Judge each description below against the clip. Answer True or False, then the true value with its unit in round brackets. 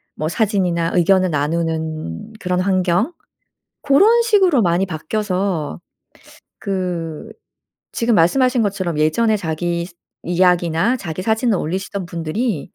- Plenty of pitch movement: False (4.6 semitones)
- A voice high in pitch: False (180 Hz)